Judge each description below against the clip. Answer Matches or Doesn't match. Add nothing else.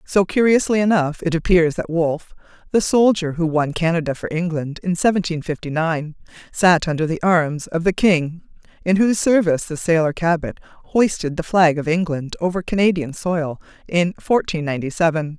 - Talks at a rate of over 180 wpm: Doesn't match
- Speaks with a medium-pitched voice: Matches